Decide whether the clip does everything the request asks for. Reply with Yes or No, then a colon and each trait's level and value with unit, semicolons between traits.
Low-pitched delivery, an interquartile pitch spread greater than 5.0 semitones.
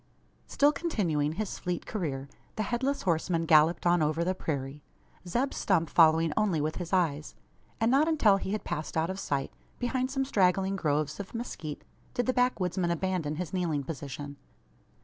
No: medium, 175 Hz; wide, 5.6 semitones